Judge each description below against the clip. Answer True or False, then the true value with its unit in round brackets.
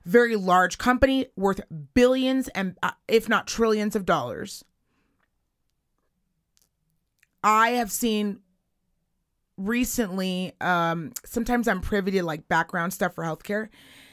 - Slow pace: True (110 wpm)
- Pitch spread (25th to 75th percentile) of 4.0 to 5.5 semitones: True (4.5 semitones)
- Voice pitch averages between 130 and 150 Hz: False (205 Hz)